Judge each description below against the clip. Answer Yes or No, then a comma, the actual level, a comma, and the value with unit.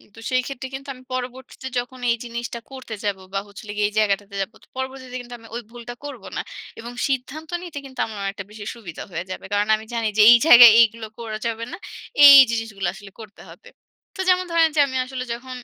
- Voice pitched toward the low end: No, high, 235 Hz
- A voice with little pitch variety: No, average, 3.2 semitones